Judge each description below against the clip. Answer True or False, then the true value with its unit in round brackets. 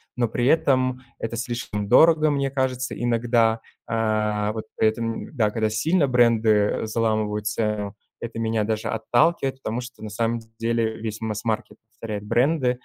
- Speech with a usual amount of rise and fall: False (2.3 semitones)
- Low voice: True (115 Hz)